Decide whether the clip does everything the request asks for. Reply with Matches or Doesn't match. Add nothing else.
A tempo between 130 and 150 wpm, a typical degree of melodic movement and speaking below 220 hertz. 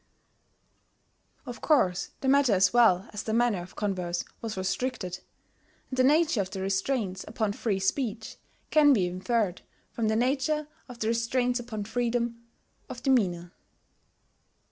Doesn't match